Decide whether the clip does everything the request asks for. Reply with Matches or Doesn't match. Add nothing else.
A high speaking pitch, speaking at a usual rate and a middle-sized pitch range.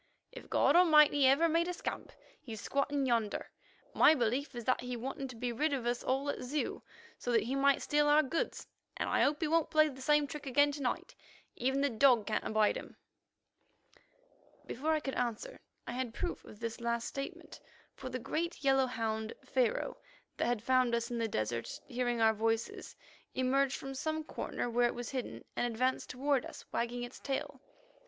Matches